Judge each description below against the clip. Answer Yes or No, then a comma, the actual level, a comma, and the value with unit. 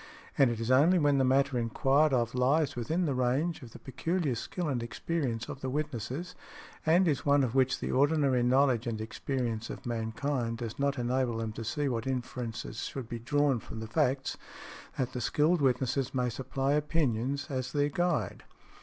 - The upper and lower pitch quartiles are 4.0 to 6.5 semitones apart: No, average, 3.3 semitones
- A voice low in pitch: Yes, low, 130 Hz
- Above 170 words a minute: Yes, average, 185 wpm